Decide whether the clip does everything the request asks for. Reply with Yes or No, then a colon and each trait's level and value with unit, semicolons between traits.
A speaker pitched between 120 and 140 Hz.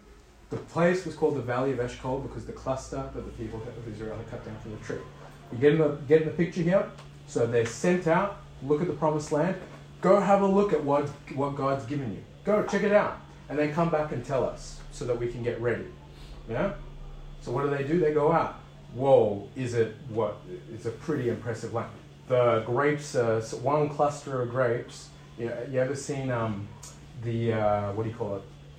Yes: low, 135 Hz